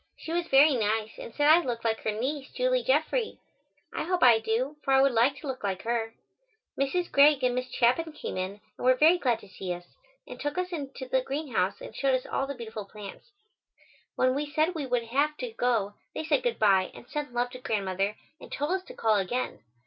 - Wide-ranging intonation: No, average, 4.9 semitones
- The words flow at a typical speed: No, fast, 225 wpm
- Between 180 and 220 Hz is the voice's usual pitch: No, very high, 255 Hz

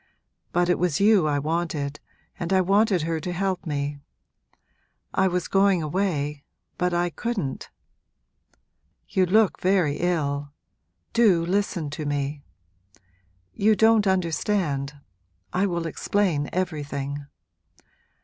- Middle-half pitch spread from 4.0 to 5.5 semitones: Yes, average, 4.7 semitones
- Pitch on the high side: No, medium, 175 Hz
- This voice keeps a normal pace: No, slow, 115 wpm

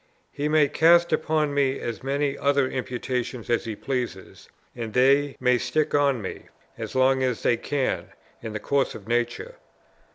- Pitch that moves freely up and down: No, average, 3.0 semitones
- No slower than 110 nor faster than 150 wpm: No, average, 165 wpm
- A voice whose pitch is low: Yes, low, 130 Hz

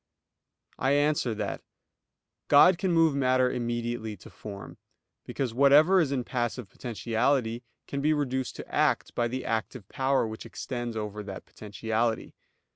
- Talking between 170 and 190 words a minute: No, average, 140 wpm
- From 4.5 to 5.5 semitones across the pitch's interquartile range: No, average, 3.8 semitones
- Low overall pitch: Yes, low, 125 Hz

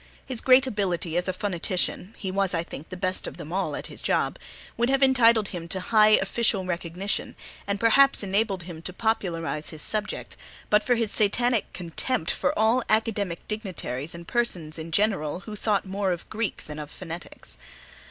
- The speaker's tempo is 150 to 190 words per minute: Yes, average, 180 wpm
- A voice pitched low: No, high, 195 Hz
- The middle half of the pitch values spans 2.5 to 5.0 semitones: Yes, average, 4.4 semitones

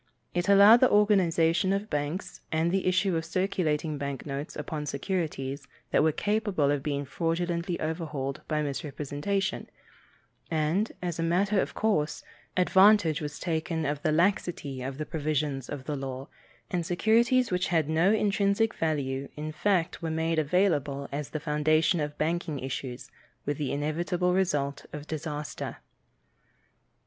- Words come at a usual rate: Yes, average, 145 wpm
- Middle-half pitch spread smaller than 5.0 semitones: Yes, average, 3.9 semitones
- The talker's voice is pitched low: No, medium, 160 Hz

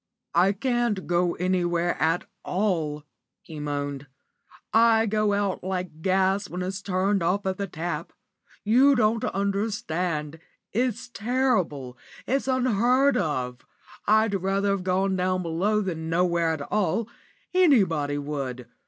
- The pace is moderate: No, slow, 125 wpm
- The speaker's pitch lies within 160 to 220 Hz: Yes, high, 190 Hz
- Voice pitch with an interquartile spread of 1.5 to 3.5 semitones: No, average, 4.4 semitones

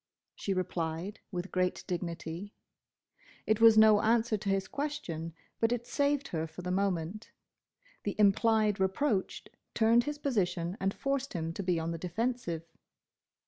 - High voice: Yes, high, 195 Hz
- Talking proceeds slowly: No, average, 145 wpm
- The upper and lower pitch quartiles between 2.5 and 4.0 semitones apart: No, average, 4.5 semitones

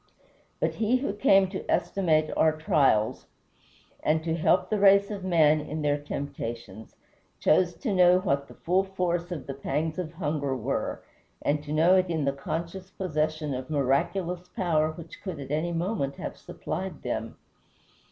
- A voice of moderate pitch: Yes, medium, 160 Hz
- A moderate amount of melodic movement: Yes, average, 4.0 semitones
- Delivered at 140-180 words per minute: Yes, average, 165 wpm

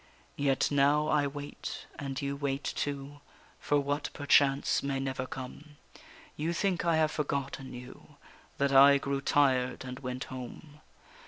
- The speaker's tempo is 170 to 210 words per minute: No, average, 145 wpm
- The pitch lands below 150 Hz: Yes, medium, 140 Hz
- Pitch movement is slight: Yes, narrow, 1.3 semitones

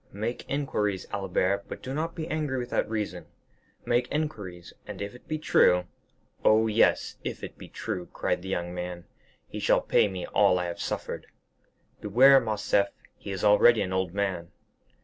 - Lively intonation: No, average, 4.8 semitones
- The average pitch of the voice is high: No, low, 105 Hz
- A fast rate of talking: No, average, 170 wpm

